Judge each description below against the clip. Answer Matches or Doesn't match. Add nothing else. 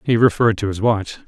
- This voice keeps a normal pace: Doesn't match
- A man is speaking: Matches